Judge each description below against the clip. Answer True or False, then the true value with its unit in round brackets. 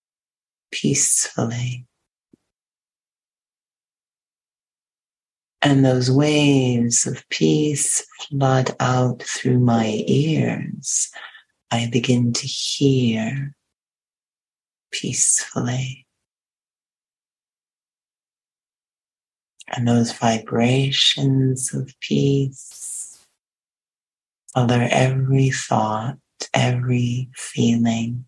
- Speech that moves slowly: True (55 wpm)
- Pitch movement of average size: False (2.3 semitones)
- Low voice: True (125 Hz)